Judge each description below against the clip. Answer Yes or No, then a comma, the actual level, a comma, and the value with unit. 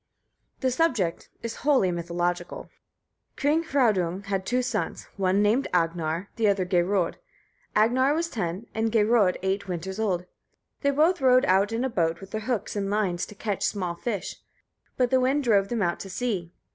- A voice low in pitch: No, high, 205 Hz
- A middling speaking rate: Yes, average, 170 wpm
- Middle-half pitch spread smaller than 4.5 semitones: No, wide, 5.4 semitones